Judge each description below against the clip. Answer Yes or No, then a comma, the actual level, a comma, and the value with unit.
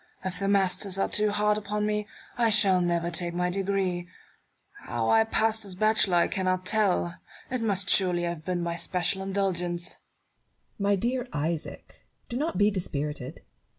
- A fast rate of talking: No, average, 165 wpm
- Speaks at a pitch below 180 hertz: No, high, 190 Hz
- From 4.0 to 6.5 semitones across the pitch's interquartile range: No, average, 3.3 semitones